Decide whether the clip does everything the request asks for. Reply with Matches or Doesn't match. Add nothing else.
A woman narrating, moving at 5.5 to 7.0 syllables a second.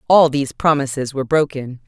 Matches